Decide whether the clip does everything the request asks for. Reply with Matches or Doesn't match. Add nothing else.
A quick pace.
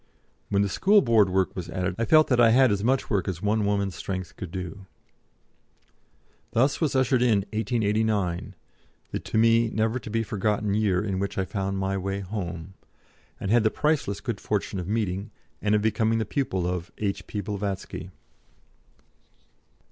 Doesn't match